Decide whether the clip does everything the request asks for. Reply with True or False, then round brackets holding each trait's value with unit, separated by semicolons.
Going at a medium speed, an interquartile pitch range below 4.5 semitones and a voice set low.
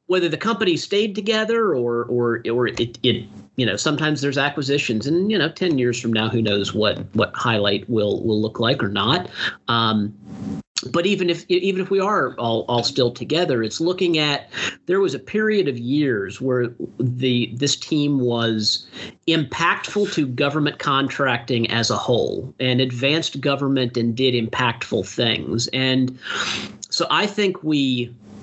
False (165 wpm; 5.0 semitones; 130 Hz)